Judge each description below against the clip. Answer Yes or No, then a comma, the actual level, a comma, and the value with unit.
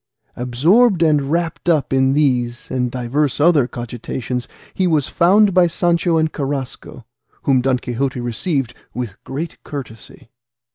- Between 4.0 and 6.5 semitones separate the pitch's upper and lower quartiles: Yes, average, 5.0 semitones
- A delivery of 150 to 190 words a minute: No, slow, 135 wpm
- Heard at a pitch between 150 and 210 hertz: No, medium, 140 Hz